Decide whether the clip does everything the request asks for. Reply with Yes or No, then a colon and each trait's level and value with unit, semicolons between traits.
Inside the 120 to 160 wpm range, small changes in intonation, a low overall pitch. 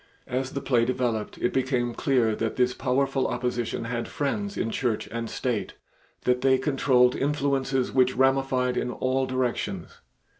Yes: average, 150 wpm; narrow, 1.6 semitones; low, 130 Hz